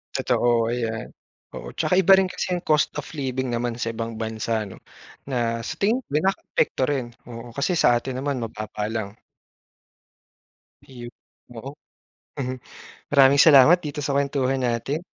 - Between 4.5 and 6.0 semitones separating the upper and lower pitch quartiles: No, average, 3.8 semitones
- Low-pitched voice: Yes, low, 130 Hz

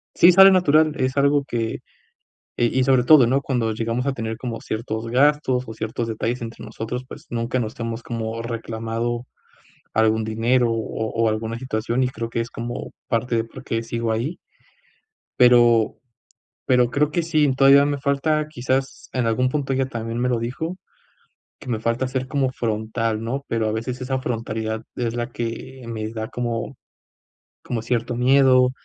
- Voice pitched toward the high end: No, low, 120 Hz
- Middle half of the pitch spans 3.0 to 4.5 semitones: No, narrow, 2.5 semitones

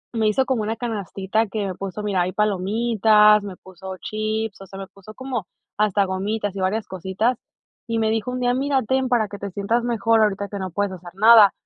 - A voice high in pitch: Yes, high, 210 Hz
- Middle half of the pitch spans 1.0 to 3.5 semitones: Yes, narrow, 2.6 semitones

